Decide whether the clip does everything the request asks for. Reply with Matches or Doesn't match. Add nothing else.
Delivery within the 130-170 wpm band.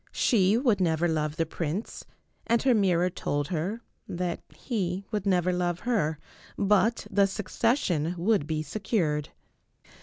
Matches